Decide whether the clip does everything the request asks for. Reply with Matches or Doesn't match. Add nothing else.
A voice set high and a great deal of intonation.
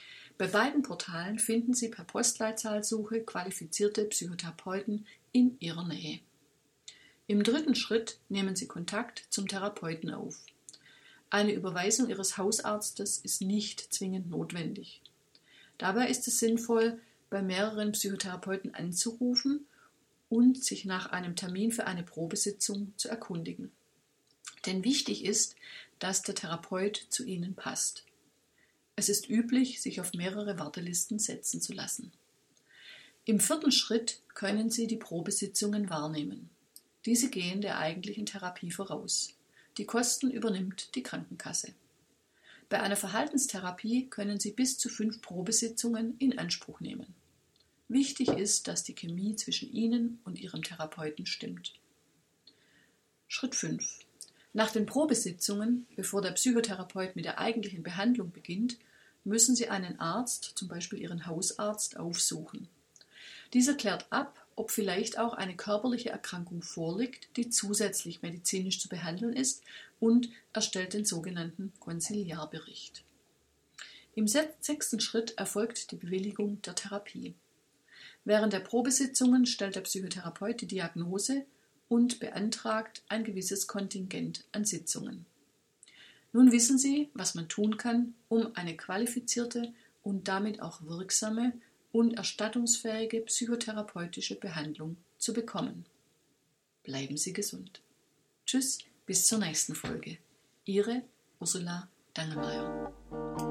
Doesn't match